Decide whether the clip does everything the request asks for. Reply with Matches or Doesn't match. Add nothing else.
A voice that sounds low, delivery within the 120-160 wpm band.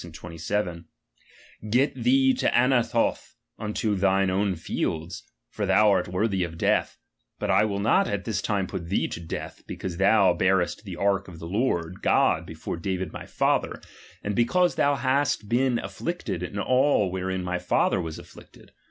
Doesn't match